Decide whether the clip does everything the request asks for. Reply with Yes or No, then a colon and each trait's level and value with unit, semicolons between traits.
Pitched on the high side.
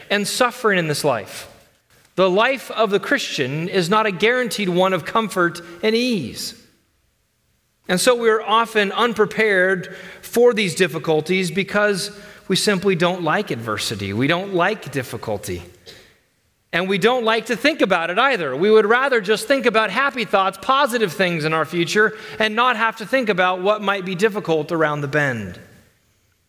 Yes: high, 195 Hz